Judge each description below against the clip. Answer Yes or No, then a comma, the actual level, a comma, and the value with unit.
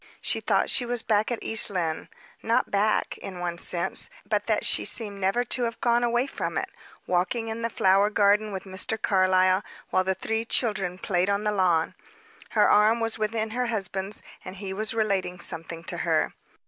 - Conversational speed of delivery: Yes, average, 190 wpm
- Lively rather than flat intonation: No, average, 3.1 semitones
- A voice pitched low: No, high, 205 Hz